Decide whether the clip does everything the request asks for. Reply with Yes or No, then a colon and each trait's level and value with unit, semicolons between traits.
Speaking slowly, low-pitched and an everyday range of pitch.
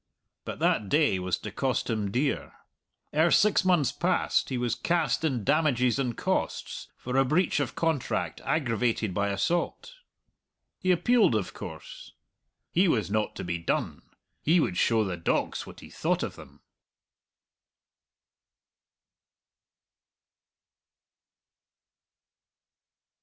No: slow, 120 wpm; low, 125 Hz; wide, 6.9 semitones